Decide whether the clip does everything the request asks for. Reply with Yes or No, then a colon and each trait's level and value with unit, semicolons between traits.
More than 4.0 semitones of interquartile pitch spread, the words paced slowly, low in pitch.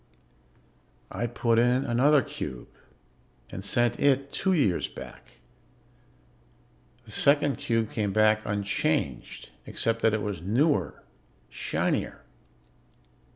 Yes: average, 5.0 semitones; slow, 105 wpm; low, 115 Hz